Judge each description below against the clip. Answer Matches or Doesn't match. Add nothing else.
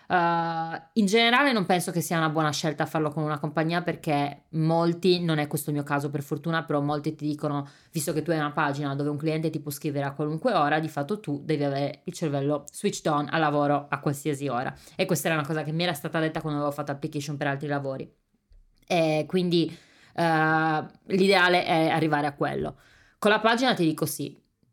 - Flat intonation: Matches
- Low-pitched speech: Doesn't match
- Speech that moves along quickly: Matches